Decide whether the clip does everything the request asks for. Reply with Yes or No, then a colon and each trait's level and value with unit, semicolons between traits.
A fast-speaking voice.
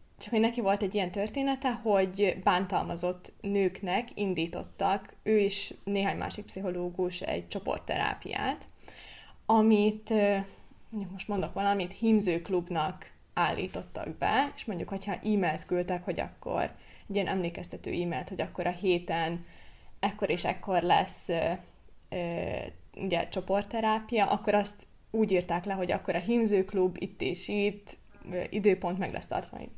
No: average, 135 wpm